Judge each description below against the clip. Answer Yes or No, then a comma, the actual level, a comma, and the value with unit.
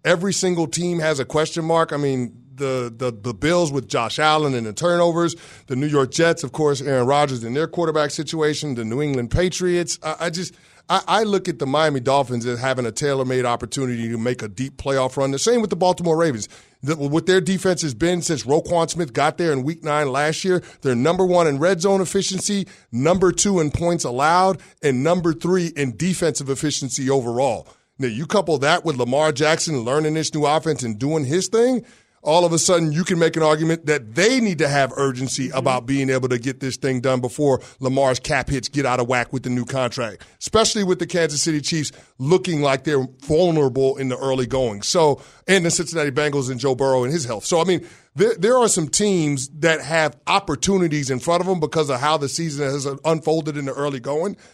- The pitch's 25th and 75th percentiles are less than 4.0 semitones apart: No, average, 4.3 semitones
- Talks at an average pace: No, fast, 220 wpm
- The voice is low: No, medium, 150 Hz